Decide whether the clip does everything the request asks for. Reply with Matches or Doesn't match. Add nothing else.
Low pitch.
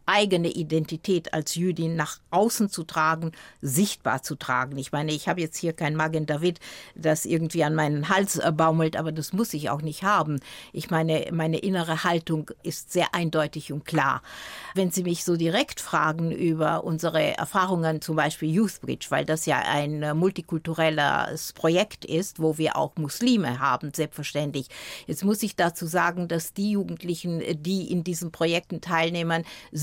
Doesn't match